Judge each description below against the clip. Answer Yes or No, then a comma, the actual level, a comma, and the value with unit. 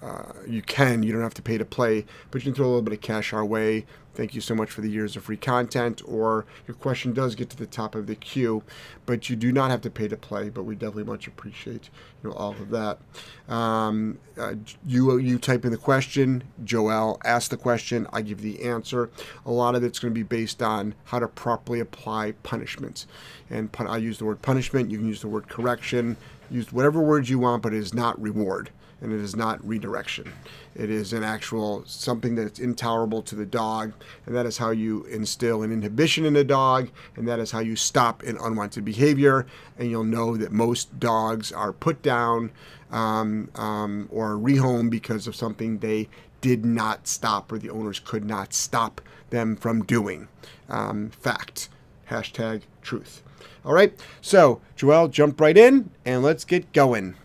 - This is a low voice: Yes, low, 115 Hz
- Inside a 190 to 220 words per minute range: Yes, average, 200 wpm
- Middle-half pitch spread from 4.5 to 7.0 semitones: No, narrow, 2.6 semitones